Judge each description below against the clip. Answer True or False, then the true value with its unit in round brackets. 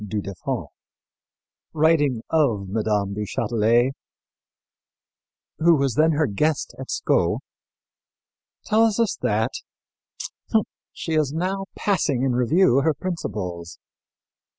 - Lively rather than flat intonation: True (7.0 semitones)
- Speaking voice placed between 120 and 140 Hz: True (135 Hz)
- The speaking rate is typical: False (105 wpm)